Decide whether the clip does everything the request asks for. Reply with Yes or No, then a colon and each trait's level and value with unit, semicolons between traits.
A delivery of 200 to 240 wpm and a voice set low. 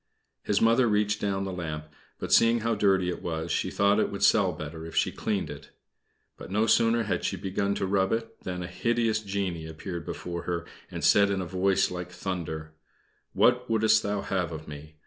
Yes: fast, 205 wpm; very low, 95 Hz